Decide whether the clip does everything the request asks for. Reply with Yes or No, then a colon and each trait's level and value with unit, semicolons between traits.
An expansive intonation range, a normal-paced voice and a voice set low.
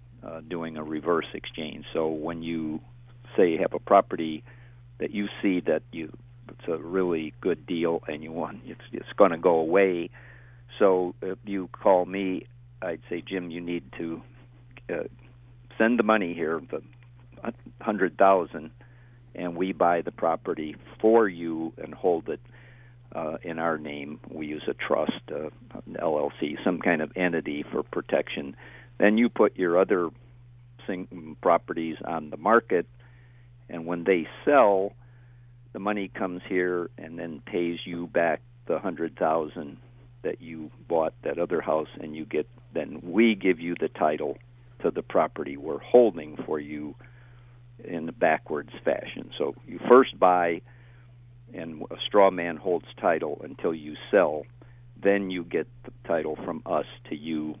Yes: wide, 6.4 semitones; average, 155 wpm; very low, 95 Hz